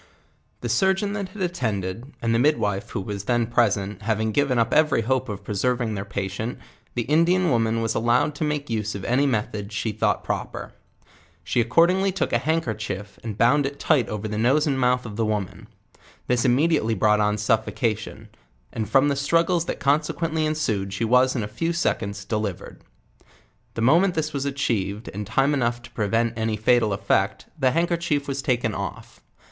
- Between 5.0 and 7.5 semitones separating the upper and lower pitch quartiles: Yes, average, 5.3 semitones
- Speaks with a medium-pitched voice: No, low, 120 Hz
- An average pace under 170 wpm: No, average, 185 wpm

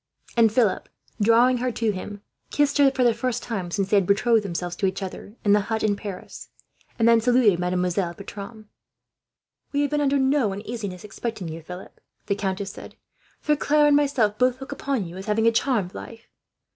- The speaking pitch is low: No, high, 220 Hz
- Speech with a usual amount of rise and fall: Yes, average, 4.4 semitones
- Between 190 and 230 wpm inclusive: Yes, average, 195 wpm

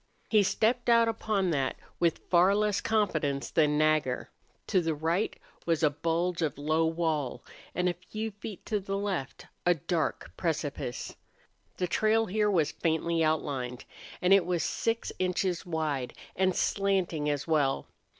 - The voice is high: No, medium, 170 Hz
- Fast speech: No, average, 150 wpm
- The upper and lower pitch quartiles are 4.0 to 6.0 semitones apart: Yes, average, 4.3 semitones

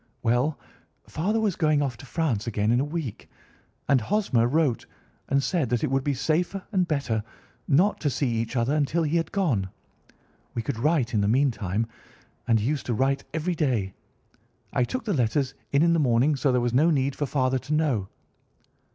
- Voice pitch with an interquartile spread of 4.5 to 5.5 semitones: Yes, average, 4.8 semitones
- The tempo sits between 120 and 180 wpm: No, average, 195 wpm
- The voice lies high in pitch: No, medium, 140 Hz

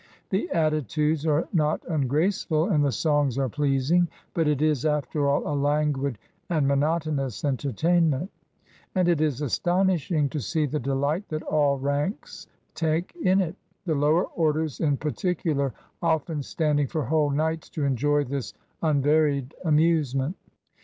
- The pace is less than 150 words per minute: Yes, average, 140 wpm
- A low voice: No, medium, 150 Hz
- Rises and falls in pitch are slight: Yes, narrow, 2.3 semitones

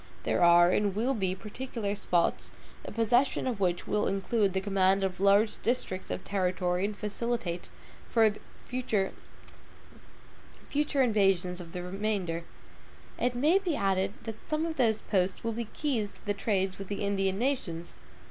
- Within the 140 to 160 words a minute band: Yes, average, 150 wpm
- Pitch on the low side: No, high, 200 Hz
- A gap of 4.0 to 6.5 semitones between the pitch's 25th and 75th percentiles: No, average, 3.6 semitones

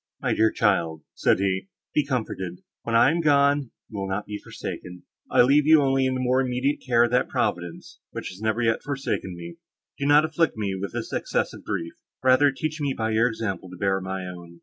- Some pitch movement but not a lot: No, wide, 6.2 semitones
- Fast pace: Yes, fast, 215 wpm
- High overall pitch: No, low, 115 Hz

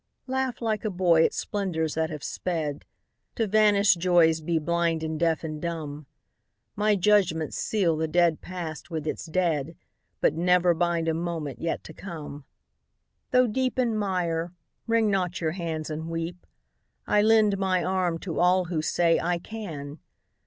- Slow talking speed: No, average, 160 wpm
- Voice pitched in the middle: Yes, medium, 170 Hz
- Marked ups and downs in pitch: No, average, 3.4 semitones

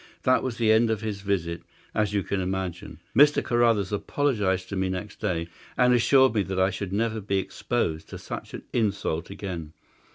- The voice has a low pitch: Yes, low, 100 Hz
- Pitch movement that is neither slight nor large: Yes, average, 3.5 semitones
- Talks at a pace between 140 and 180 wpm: No, average, 190 wpm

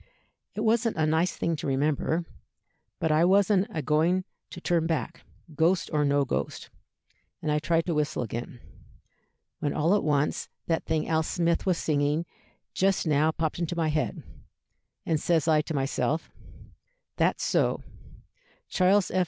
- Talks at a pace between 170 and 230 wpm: No, average, 155 wpm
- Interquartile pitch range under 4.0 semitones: Yes, narrow, 2.5 semitones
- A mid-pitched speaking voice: Yes, medium, 160 Hz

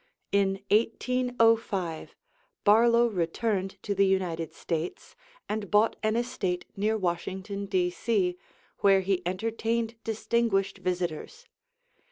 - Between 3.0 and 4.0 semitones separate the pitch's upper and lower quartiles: Yes, average, 3.6 semitones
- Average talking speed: No, slow, 100 wpm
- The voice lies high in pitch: Yes, high, 200 Hz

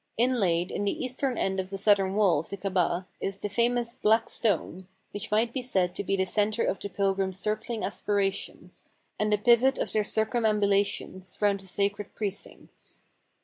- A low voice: No, high, 205 Hz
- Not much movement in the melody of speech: Yes, narrow, 2.3 semitones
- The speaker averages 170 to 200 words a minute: Yes, average, 185 wpm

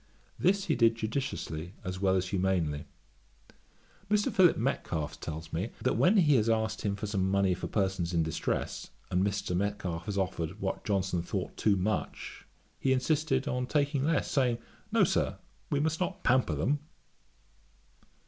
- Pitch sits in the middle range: No, low, 100 Hz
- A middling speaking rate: Yes, average, 165 wpm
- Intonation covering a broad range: Yes, wide, 6.3 semitones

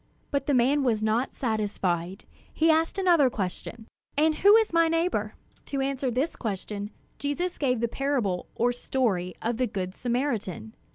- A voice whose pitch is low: No, very high, 250 Hz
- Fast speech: No, average, 160 wpm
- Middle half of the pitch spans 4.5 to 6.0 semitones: Yes, wide, 5.5 semitones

